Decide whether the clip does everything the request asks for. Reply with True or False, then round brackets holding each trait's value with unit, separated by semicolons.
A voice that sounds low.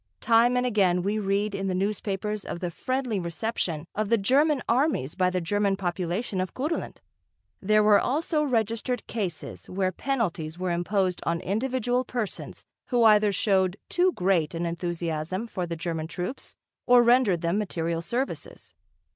False (200 Hz)